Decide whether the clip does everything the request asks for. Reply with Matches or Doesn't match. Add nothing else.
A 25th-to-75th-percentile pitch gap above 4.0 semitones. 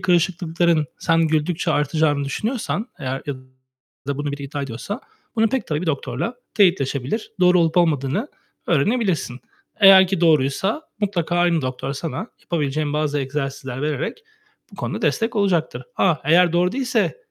Matches